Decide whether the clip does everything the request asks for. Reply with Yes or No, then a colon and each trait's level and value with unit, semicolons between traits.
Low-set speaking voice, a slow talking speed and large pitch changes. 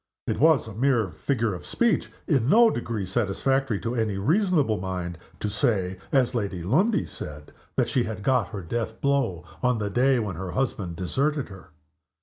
No: low, 115 Hz; average, 175 wpm; wide, 5.8 semitones